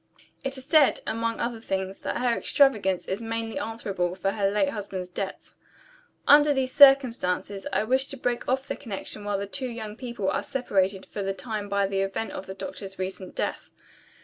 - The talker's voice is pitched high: Yes, high, 215 Hz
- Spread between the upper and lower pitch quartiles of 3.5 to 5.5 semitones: Yes, average, 4.8 semitones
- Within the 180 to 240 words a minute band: Yes, average, 190 wpm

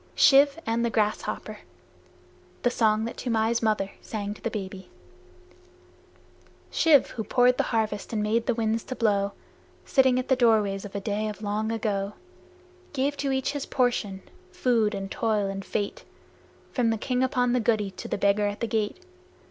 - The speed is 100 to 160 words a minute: No, average, 170 wpm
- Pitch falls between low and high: No, high, 220 Hz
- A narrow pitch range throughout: No, average, 3.1 semitones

